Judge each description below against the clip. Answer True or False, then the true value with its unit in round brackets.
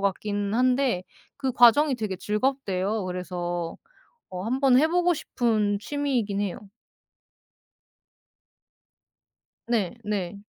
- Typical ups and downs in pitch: True (5.0 semitones)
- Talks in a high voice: True (210 Hz)